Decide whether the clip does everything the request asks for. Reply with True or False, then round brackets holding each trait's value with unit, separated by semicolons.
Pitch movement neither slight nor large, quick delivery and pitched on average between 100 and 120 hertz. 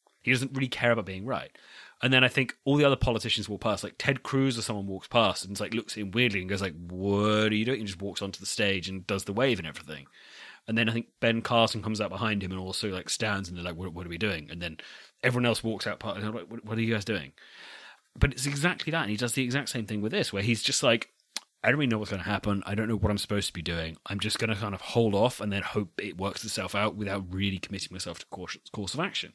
True (3.1 semitones; 295 wpm; 105 Hz)